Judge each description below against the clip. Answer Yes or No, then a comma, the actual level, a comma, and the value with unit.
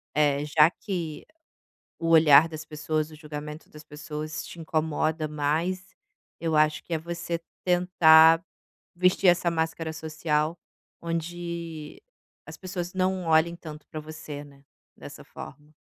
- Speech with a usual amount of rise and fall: No, narrow, 1.9 semitones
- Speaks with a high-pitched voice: No, medium, 160 Hz